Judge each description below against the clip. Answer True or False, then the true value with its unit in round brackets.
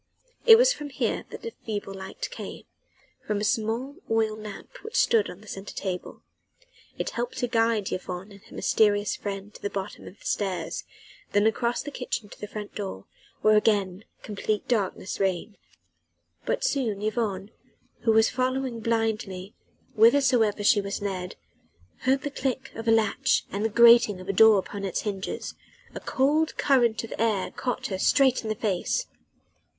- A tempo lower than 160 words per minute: False (170 wpm)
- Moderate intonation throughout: True (3.3 semitones)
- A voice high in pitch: True (215 Hz)